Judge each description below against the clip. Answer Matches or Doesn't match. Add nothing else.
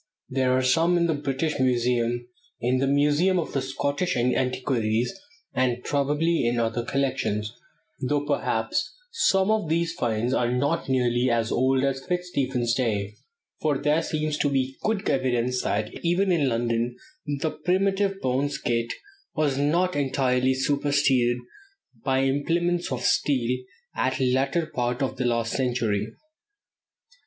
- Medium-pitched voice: Doesn't match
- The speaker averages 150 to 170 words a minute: Doesn't match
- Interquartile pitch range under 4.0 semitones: Matches